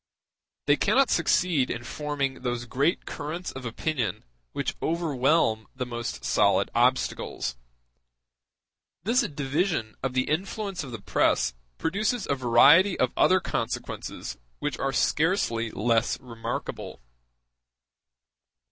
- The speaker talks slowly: Yes, slow, 110 wpm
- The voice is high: No, low, 135 Hz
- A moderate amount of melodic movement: No, wide, 5.9 semitones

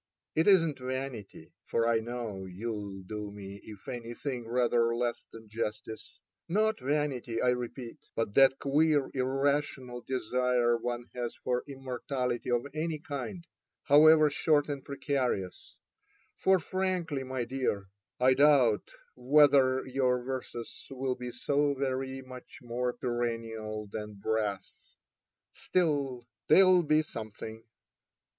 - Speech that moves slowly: Yes, slow, 125 wpm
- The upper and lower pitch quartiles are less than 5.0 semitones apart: Yes, average, 3.4 semitones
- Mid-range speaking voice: No, low, 125 Hz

